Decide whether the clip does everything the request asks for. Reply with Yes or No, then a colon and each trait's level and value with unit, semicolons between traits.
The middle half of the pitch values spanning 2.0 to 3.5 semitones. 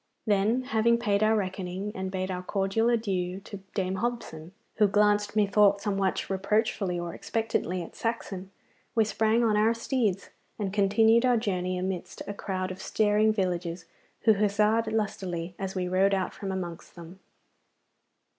Yes: average, 2.7 semitones